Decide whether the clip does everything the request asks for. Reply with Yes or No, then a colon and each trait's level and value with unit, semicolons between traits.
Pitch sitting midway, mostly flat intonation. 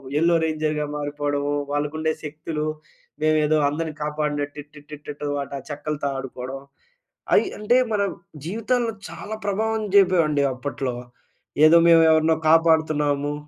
Yes: medium, 155 Hz; narrow, 2.0 semitones